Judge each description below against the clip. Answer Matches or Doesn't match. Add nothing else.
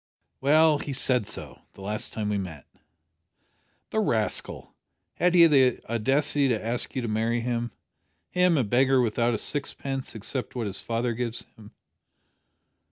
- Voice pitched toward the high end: Doesn't match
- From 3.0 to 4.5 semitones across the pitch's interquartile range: Matches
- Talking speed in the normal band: Matches